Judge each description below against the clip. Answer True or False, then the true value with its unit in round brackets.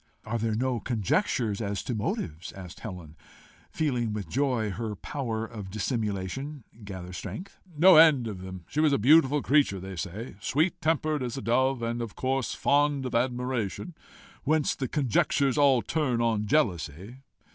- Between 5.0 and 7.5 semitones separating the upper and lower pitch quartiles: True (5.4 semitones)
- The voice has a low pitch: True (120 Hz)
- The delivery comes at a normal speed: True (160 wpm)